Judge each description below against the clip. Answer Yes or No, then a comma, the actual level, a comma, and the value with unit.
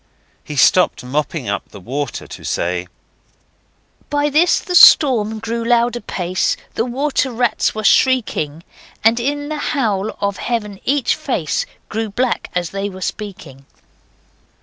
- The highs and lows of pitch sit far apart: Yes, wide, 6.4 semitones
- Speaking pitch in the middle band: No, high, 220 Hz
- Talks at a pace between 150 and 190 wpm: No, average, 140 wpm